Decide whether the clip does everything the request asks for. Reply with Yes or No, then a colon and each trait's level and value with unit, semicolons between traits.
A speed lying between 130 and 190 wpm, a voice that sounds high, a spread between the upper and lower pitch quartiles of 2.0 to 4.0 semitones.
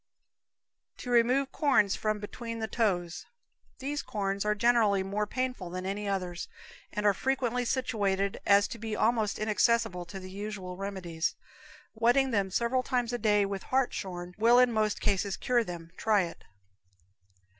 Yes: average, 155 wpm; high, 210 Hz; average, 3.5 semitones